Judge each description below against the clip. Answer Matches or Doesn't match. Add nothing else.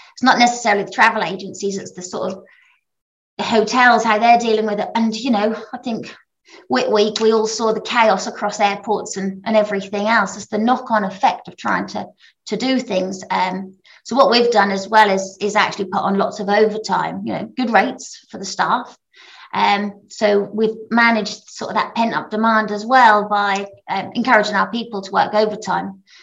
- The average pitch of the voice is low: Doesn't match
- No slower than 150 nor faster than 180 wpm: Doesn't match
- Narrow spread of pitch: Matches